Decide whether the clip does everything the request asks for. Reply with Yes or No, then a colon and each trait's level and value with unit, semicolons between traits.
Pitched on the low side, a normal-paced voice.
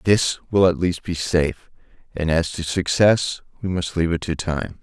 Yes: very low, 85 Hz; average, 185 wpm